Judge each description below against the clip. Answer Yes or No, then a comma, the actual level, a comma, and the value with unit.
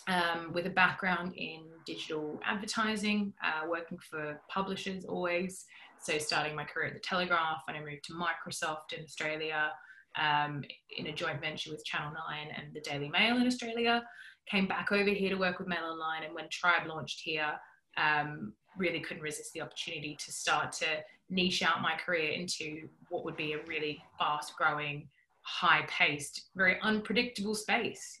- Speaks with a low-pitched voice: No, medium, 165 Hz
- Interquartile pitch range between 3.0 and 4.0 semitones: Yes, average, 3.3 semitones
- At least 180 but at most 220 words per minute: No, average, 170 wpm